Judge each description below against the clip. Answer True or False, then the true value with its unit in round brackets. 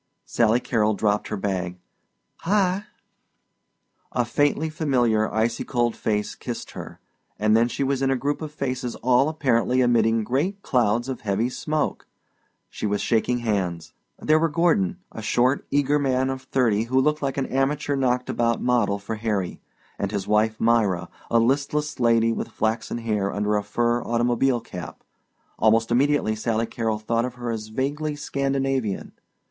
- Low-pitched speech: True (120 Hz)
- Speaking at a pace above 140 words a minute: True (160 wpm)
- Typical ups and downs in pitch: True (3.8 semitones)